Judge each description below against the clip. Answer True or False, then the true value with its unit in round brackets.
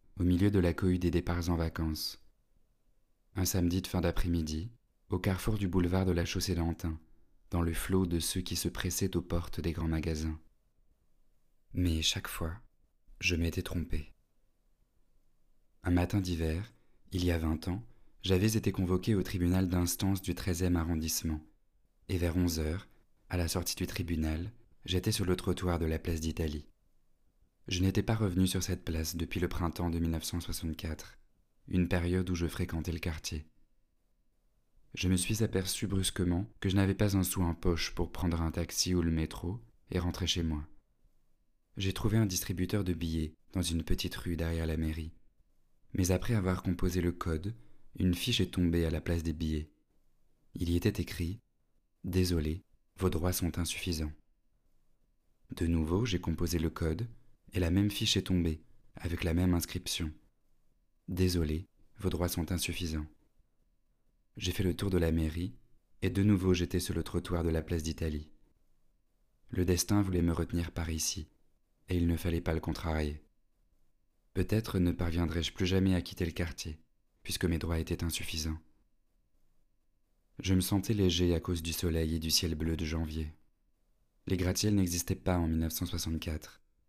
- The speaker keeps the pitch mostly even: True (2.2 semitones)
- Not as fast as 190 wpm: True (165 wpm)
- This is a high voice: False (85 Hz)